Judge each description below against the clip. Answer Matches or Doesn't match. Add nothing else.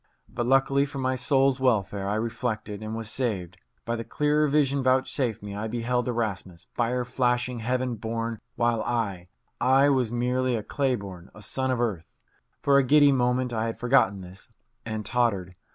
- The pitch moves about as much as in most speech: Matches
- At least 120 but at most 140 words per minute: Doesn't match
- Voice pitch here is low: Matches